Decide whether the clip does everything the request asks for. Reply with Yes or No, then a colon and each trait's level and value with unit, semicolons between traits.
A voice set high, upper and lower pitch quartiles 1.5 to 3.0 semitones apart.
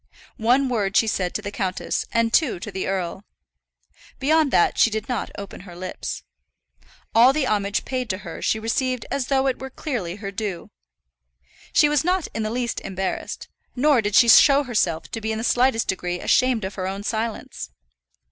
No: high, 225 Hz; average, 4.8 semitones